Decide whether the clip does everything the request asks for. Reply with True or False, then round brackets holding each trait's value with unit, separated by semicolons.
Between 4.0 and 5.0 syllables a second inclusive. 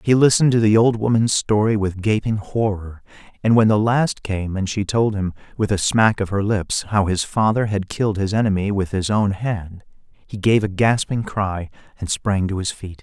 True (4.9 syllables/s)